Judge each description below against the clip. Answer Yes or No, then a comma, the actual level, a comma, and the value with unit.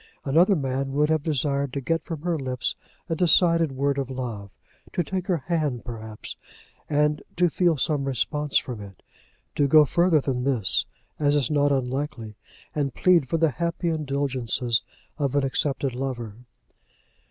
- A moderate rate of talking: Yes, average, 160 wpm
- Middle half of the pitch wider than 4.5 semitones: No, average, 3.4 semitones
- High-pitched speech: No, medium, 140 Hz